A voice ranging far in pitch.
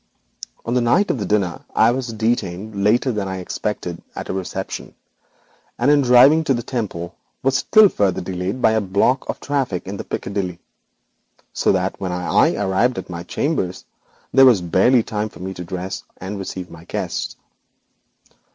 No: average, 4.9 semitones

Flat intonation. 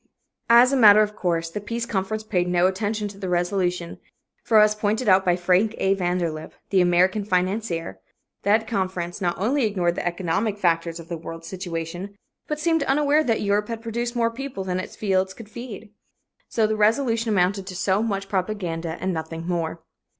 No: average, 3.6 semitones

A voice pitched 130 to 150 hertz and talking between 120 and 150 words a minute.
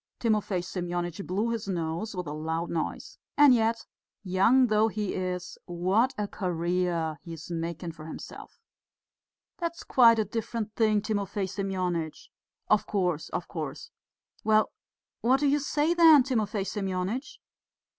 No: high, 195 Hz; average, 140 wpm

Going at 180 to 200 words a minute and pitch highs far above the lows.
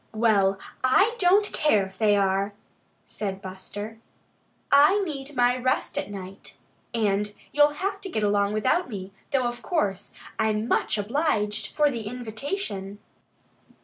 No: average, 140 wpm; wide, 6.1 semitones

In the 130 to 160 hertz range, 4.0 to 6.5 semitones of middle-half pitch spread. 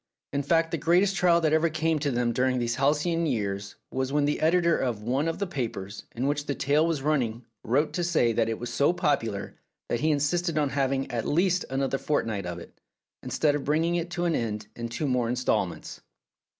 Yes: medium, 140 Hz; average, 5.2 semitones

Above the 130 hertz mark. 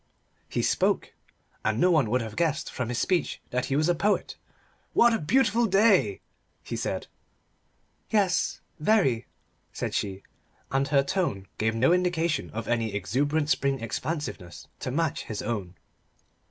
Yes: medium, 140 Hz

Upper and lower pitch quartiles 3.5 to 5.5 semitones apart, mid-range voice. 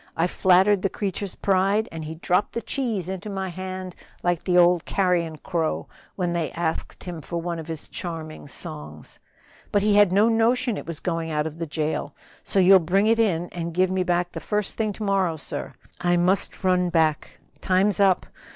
No: average, 2.9 semitones; medium, 180 Hz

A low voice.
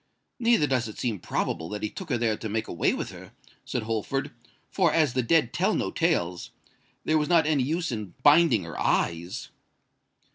Yes: low, 125 Hz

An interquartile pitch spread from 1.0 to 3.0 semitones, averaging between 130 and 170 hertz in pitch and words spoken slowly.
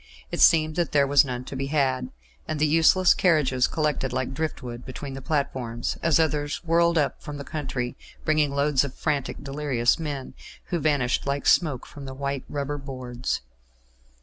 No: average, 2.7 semitones; medium, 140 Hz; average, 175 wpm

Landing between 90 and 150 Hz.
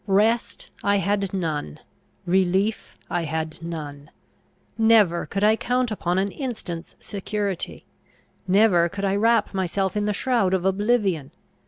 No: high, 195 Hz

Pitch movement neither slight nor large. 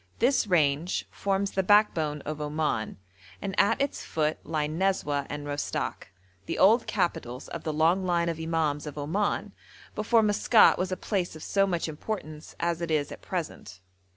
Yes: average, 4.5 semitones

